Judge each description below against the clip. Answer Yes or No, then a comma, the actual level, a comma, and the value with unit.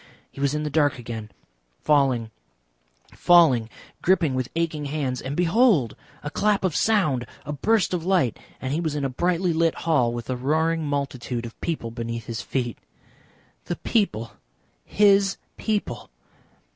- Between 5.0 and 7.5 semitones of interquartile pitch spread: Yes, wide, 5.6 semitones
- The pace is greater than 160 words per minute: No, average, 155 wpm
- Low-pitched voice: No, medium, 145 Hz